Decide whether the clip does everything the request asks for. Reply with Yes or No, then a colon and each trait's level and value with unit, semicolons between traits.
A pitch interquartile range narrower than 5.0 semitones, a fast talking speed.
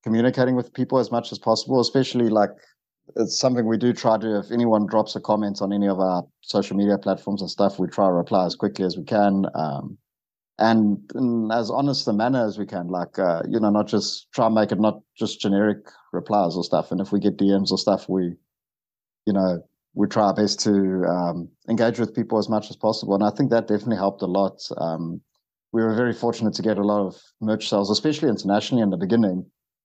Yes: average, 2.7 semitones; fast, 225 wpm